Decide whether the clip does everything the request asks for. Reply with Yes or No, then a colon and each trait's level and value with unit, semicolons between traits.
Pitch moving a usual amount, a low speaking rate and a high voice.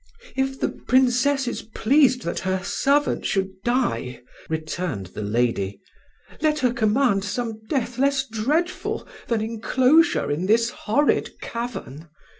No: wide, 6.1 semitones; slow, 125 wpm; high, 235 Hz